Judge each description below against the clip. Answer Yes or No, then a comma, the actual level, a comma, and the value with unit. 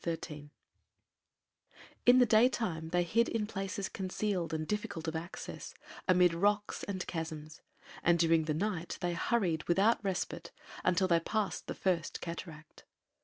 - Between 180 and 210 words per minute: No, average, 140 wpm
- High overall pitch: No, medium, 175 Hz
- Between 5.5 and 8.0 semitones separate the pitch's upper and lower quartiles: No, average, 3.9 semitones